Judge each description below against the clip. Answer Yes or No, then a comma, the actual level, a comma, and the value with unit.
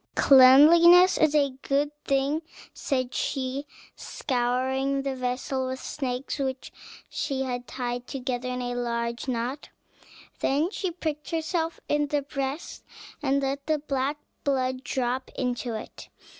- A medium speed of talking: No, slow, 130 wpm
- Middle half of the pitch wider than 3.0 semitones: No, narrow, 2.4 semitones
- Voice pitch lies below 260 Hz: No, very high, 270 Hz